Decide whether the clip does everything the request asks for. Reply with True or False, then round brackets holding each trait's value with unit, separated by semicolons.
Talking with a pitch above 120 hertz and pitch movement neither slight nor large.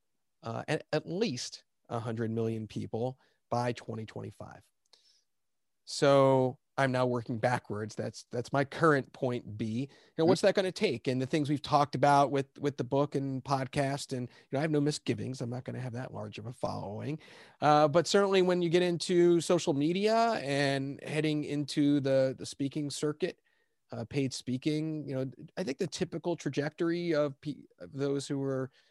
True (140 Hz; 3.4 semitones)